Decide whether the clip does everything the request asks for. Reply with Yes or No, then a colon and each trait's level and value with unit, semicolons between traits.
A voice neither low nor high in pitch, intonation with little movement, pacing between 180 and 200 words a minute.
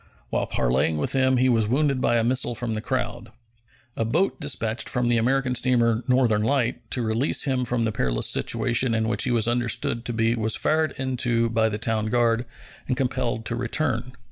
No: low, 120 Hz; narrow, 2.3 semitones; average, 195 wpm